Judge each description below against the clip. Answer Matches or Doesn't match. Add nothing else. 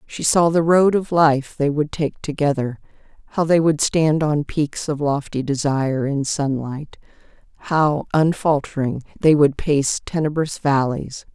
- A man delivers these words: Doesn't match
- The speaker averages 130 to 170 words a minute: Matches